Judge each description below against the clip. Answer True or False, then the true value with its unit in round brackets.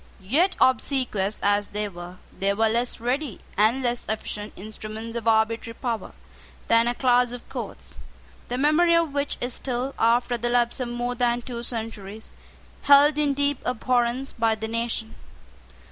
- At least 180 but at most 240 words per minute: False (160 wpm)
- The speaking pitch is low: False (240 Hz)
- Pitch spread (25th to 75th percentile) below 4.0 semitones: True (2.6 semitones)